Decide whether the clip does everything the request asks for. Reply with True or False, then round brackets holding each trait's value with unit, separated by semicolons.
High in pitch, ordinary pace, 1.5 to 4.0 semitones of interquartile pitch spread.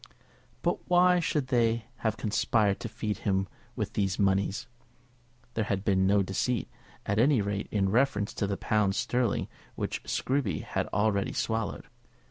False (105 Hz; 150 wpm; 3.0 semitones)